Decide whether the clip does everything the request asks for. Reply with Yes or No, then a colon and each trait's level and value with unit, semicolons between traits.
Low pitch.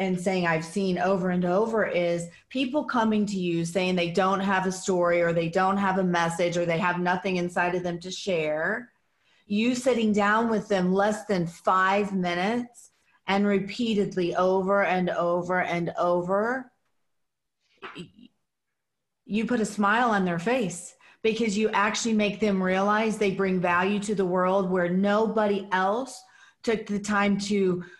No: high, 195 Hz